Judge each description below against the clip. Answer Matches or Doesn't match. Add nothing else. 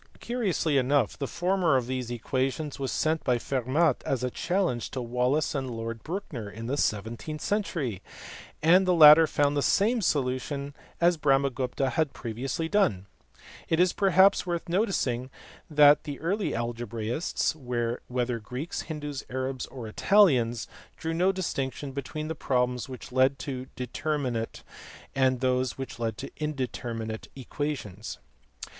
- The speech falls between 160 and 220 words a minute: Doesn't match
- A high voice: Doesn't match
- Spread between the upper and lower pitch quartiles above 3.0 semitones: Matches